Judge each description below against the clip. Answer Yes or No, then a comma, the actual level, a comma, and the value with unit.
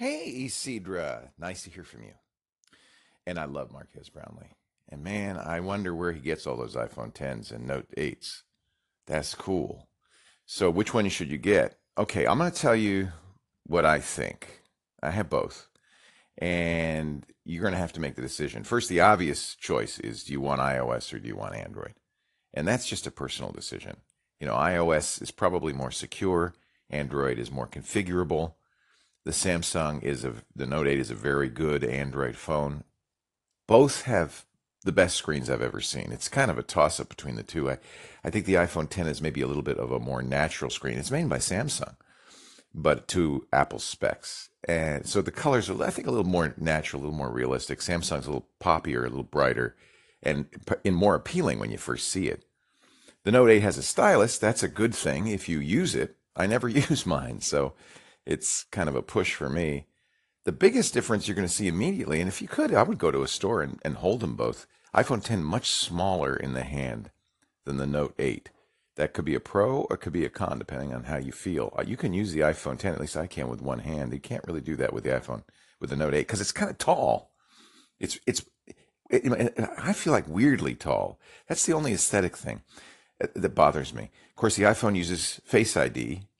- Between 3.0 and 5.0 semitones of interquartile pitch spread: No, wide, 5.6 semitones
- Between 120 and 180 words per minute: No, fast, 205 wpm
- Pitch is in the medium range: No, very low, 80 Hz